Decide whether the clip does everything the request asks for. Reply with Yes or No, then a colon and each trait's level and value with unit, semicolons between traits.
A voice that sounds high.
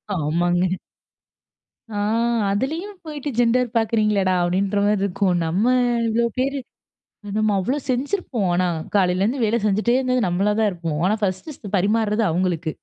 Yes: high, 210 Hz